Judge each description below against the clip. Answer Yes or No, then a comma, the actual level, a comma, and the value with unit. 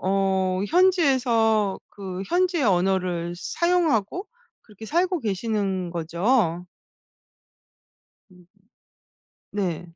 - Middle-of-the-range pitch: No, high, 200 Hz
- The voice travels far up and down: Yes, wide, 6.4 semitones